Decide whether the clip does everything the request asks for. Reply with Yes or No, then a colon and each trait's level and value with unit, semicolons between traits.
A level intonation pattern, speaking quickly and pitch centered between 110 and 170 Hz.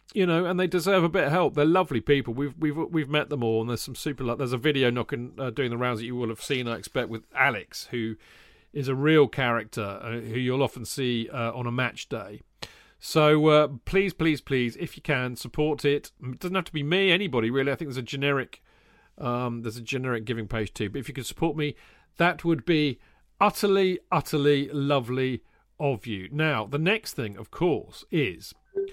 No: average, 4.5 semitones; fast, 220 wpm; medium, 140 Hz